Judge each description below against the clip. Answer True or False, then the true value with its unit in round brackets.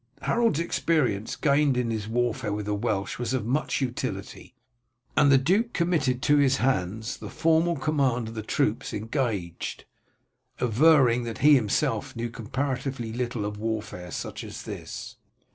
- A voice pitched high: False (125 Hz)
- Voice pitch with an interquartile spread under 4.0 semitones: False (4.6 semitones)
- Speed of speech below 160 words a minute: True (150 wpm)